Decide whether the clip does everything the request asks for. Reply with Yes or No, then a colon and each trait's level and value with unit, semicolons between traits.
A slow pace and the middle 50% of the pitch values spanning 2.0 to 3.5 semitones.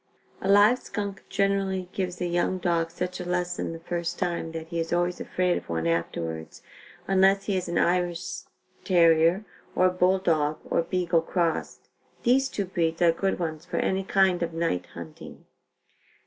No: average, 170 wpm; narrow, 2.4 semitones